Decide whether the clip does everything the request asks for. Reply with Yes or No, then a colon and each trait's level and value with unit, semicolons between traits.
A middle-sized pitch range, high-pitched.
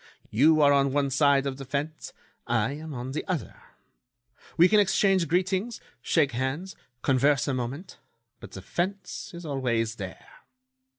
No: average, 4.7 semitones; medium, 145 Hz